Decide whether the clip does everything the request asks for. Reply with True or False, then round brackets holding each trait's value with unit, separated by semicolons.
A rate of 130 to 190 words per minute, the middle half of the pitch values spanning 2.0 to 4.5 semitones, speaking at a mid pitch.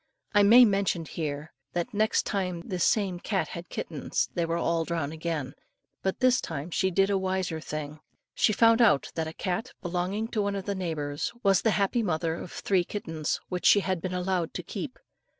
False (200 wpm; 3.6 semitones; 180 Hz)